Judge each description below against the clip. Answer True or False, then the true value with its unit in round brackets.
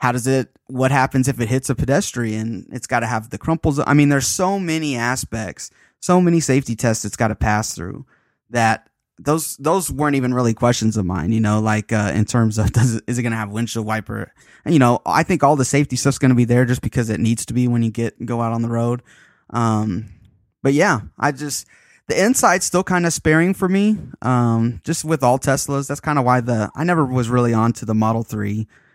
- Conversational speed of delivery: False (235 wpm)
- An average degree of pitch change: True (4.1 semitones)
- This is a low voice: True (125 Hz)